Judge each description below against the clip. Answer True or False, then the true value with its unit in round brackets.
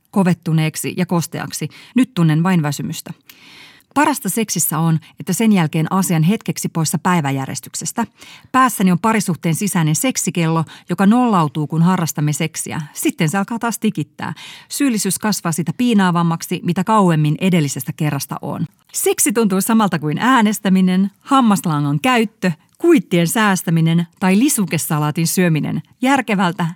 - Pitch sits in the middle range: True (180 Hz)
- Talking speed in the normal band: True (120 wpm)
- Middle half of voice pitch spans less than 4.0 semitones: False (4.6 semitones)